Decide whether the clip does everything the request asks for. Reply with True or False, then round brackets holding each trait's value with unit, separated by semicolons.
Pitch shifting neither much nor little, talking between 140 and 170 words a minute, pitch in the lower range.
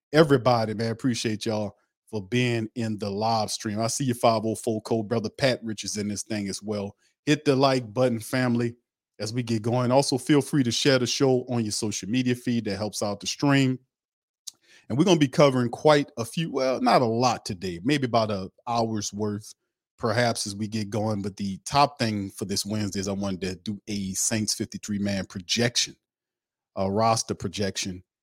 False (3.5 semitones; 200 wpm; 115 Hz)